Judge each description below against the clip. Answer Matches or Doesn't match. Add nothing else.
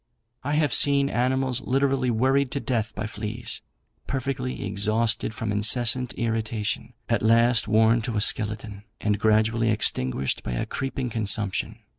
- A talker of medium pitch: Doesn't match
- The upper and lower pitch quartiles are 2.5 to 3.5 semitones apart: Matches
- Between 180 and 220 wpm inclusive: Doesn't match